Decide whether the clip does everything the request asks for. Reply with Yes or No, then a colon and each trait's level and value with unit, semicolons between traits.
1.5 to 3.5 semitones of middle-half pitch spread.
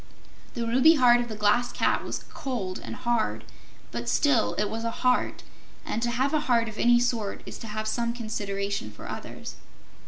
Yes: narrow, 2.5 semitones